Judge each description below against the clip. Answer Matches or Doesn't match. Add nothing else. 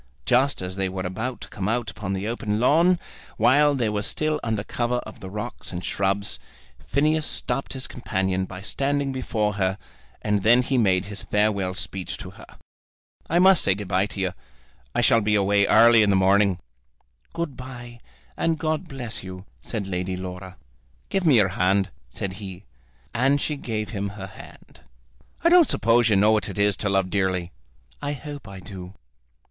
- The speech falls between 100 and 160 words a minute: Doesn't match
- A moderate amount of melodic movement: Matches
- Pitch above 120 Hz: Doesn't match